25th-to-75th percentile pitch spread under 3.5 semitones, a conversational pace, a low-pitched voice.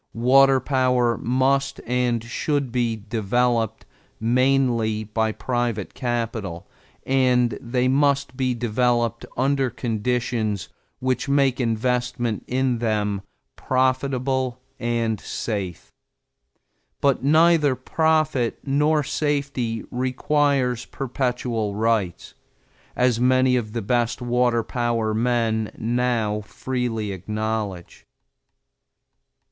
No: narrow, 2.6 semitones; slow, 90 wpm; low, 125 Hz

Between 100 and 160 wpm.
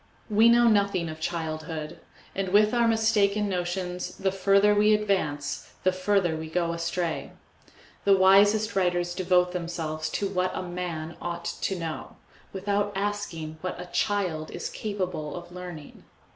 Yes: average, 145 wpm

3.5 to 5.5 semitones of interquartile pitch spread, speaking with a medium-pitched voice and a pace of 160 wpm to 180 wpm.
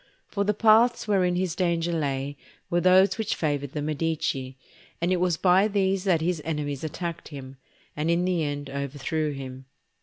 Yes: average, 4.2 semitones; medium, 165 Hz; average, 175 wpm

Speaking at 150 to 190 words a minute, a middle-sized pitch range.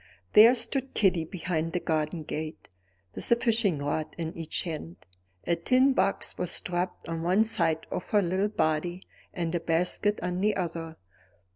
Yes: average, 165 wpm; average, 4.0 semitones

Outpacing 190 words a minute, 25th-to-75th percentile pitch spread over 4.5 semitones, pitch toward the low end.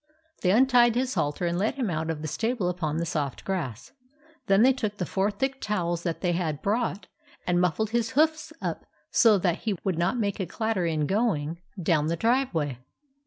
No: average, 200 wpm; wide, 5.4 semitones; high, 190 Hz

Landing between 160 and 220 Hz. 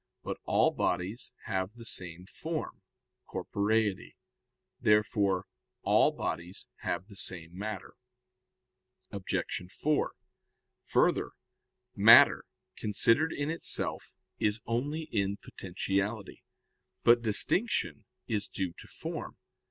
No: low, 105 Hz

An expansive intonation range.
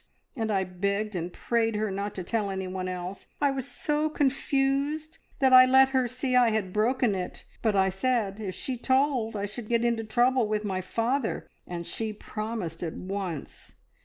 No: average, 4.8 semitones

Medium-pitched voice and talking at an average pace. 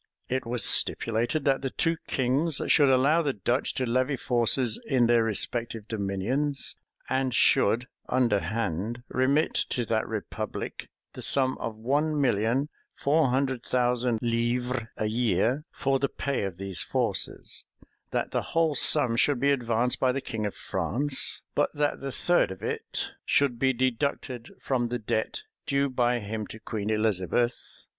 No: low, 125 Hz; average, 155 wpm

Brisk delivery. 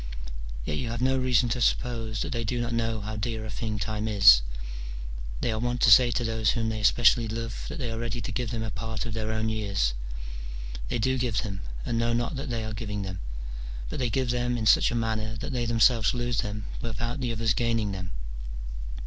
Yes: fast, 225 wpm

